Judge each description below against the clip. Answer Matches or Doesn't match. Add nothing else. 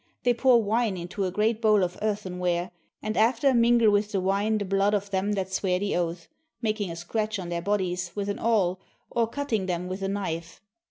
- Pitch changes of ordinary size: Matches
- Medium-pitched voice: Doesn't match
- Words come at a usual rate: Doesn't match